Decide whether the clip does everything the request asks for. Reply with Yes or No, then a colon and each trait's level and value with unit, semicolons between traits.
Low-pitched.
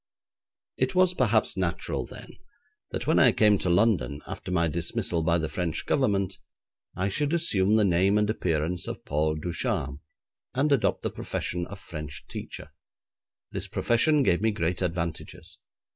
Yes: very low, 90 Hz